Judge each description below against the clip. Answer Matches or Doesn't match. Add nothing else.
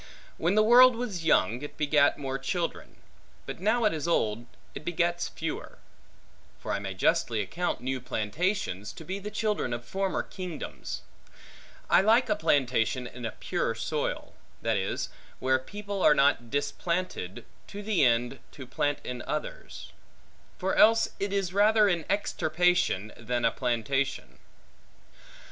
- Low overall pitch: Doesn't match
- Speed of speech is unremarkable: Matches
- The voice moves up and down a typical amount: Doesn't match